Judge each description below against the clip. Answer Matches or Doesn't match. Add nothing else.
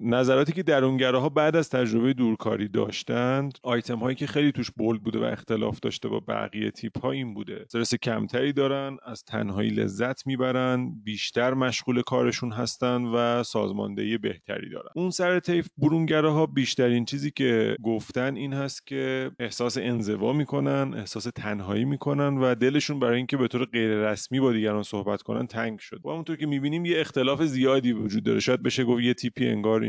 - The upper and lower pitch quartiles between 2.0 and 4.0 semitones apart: Matches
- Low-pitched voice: Matches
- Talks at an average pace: Doesn't match